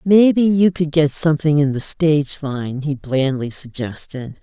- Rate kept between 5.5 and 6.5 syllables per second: No, 4.4 syllables/s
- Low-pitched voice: No, medium, 150 Hz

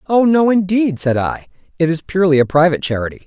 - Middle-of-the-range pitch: Yes, medium, 170 Hz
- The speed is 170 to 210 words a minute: Yes, average, 200 wpm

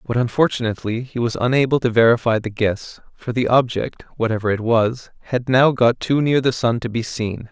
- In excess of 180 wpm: Yes, average, 200 wpm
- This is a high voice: No, low, 120 Hz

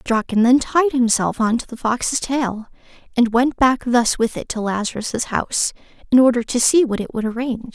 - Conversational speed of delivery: No, fast, 210 wpm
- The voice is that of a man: No, female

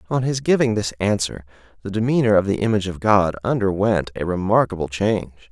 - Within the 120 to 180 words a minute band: Yes, average, 175 wpm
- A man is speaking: Yes, male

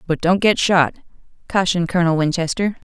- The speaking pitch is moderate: Yes, medium, 175 Hz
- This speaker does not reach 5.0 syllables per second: No, 6.1 syllables/s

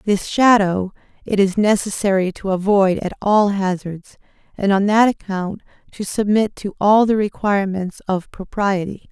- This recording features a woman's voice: Yes, female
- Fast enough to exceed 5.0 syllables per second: No, 4.5 syllables/s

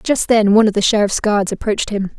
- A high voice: Yes, high, 210 Hz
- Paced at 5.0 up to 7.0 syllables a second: Yes, 6.4 syllables/s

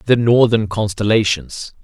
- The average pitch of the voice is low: Yes, low, 110 Hz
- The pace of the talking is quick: No, slow, 100 wpm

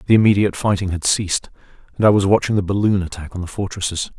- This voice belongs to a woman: No, male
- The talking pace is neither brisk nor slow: No, fast, 215 wpm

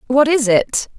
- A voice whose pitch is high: Yes, very high, 260 Hz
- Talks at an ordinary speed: Yes, average, 180 wpm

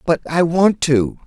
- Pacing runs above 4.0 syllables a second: No, 3.9 syllables/s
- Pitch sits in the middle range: Yes, medium, 160 Hz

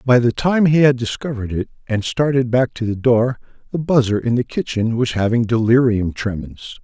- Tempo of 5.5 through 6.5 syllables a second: No, 5.2 syllables/s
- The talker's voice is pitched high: No, low, 120 Hz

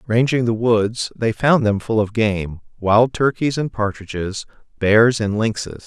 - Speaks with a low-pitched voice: Yes, low, 115 Hz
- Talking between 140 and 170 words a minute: Yes, average, 165 wpm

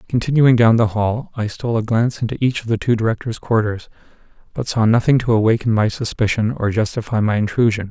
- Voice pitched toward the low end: Yes, low, 115 Hz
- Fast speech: No, average, 195 wpm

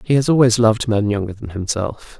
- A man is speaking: Yes, male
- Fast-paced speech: Yes, fast, 220 wpm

